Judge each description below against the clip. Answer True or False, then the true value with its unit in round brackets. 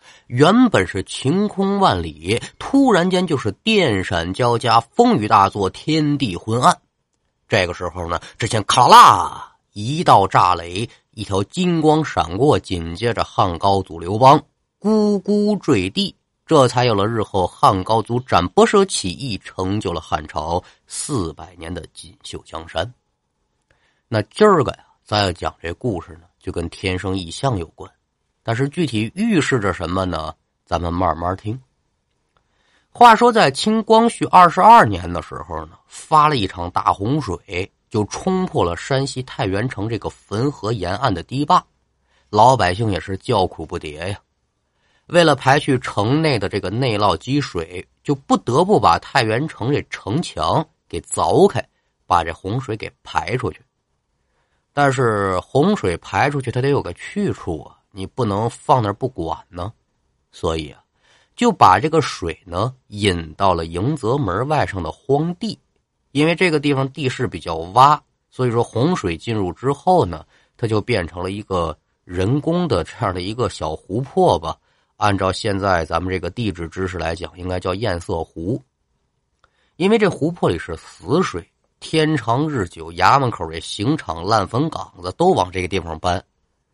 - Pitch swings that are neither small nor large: False (7.9 semitones)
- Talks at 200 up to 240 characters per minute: True (230 characters per minute)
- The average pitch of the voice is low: True (110 Hz)